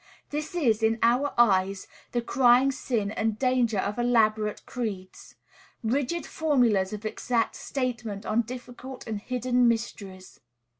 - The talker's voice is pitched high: Yes, high, 235 Hz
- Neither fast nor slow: No, slow, 130 wpm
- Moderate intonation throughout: Yes, average, 3.0 semitones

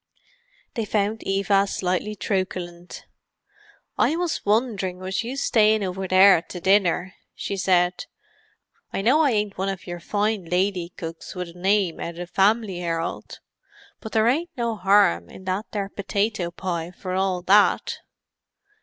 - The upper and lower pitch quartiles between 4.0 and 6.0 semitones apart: No, average, 2.9 semitones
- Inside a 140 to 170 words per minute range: Yes, average, 155 wpm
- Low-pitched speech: No, high, 195 Hz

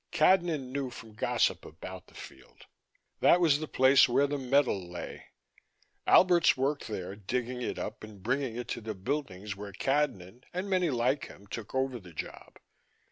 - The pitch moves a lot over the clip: Yes, wide, 5.8 semitones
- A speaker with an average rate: Yes, average, 170 wpm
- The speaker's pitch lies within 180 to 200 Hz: No, low, 125 Hz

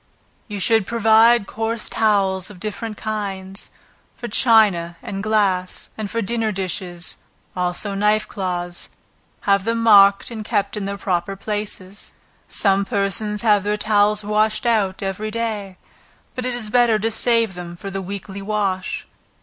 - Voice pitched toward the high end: Yes, high, 205 Hz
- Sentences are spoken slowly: No, average, 150 wpm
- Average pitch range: No, narrow, 2.2 semitones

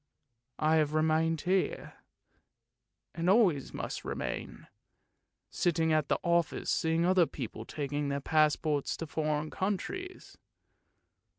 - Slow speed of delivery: Yes, slow, 110 wpm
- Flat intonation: Yes, narrow, 2.3 semitones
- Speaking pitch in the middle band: Yes, medium, 160 Hz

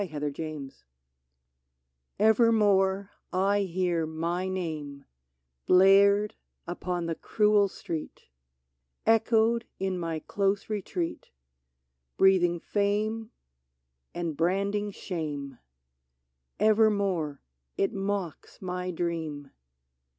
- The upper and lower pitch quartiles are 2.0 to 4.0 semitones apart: Yes, average, 3.5 semitones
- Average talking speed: No, slow, 85 wpm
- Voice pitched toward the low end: No, medium, 185 Hz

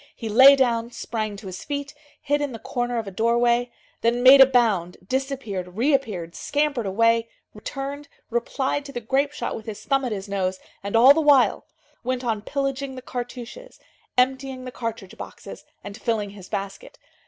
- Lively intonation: No, average, 4.0 semitones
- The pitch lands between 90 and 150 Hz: No, high, 240 Hz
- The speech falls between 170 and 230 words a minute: Yes, average, 175 wpm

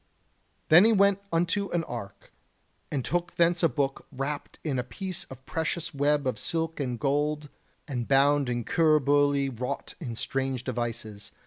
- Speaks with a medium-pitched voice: Yes, medium, 145 Hz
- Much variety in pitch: No, average, 4.3 semitones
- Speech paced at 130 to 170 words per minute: Yes, average, 160 wpm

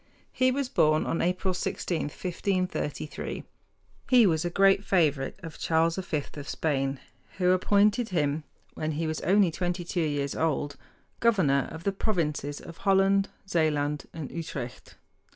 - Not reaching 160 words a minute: Yes, average, 145 wpm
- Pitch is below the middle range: No, medium, 165 Hz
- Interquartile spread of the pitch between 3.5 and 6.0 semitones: Yes, average, 4.4 semitones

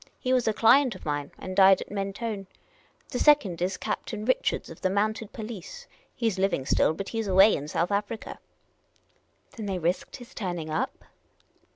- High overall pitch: Yes, high, 200 Hz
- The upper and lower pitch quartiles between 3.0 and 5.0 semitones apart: Yes, average, 3.5 semitones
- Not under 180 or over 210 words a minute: Yes, average, 195 wpm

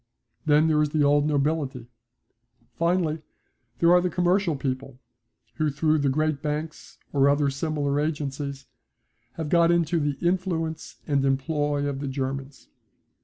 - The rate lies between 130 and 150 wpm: Yes, average, 140 wpm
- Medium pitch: Yes, medium, 150 Hz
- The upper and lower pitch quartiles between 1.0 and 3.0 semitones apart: Yes, narrow, 2.4 semitones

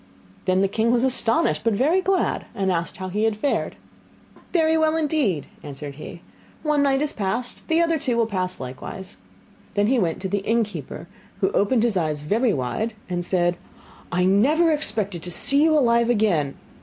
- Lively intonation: Yes, wide, 6.9 semitones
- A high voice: Yes, high, 215 Hz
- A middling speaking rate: Yes, average, 180 wpm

